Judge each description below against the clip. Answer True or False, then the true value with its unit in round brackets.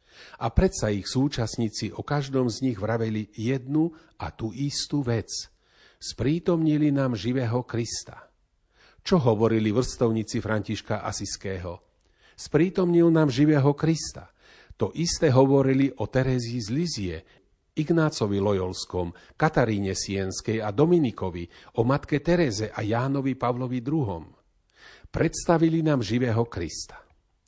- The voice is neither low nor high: False (120 Hz)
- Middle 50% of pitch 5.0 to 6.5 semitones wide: True (5.5 semitones)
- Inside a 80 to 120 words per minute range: True (110 wpm)